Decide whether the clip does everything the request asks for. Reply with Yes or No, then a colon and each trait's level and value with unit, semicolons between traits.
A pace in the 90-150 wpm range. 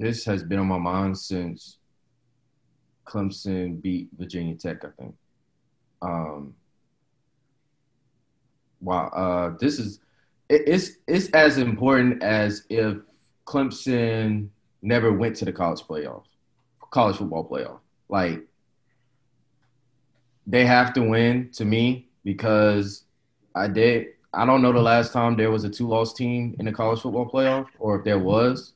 Yes: average, 140 wpm